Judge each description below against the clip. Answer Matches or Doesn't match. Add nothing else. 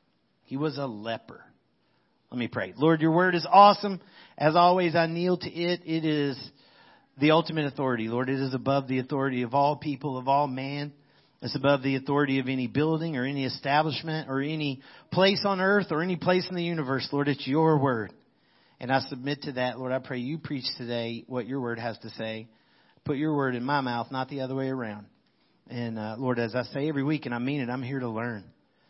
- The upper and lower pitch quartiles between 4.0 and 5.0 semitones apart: Doesn't match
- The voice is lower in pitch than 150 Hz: Matches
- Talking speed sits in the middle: Doesn't match